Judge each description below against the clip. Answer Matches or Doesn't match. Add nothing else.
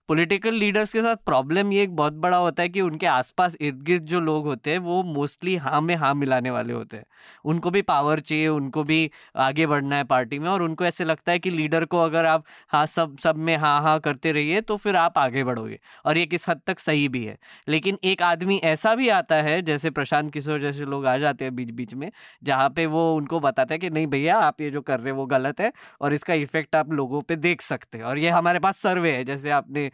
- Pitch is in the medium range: Matches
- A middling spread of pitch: Matches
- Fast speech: Matches